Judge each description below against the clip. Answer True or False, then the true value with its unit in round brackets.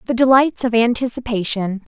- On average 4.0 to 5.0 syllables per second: False (5.3 syllables/s)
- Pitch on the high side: True (235 Hz)